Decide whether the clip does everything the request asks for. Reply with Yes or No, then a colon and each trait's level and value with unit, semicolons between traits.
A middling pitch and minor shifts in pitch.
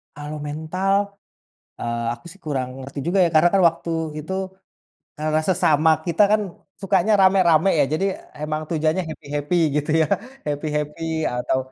No: medium, 155 Hz; average, 3.4 semitones